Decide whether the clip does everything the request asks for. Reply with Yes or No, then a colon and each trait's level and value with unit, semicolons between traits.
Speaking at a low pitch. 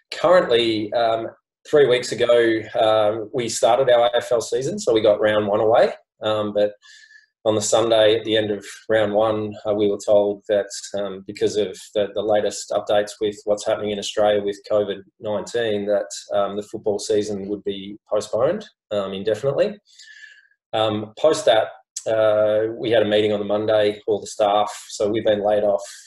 Yes: low, 105 Hz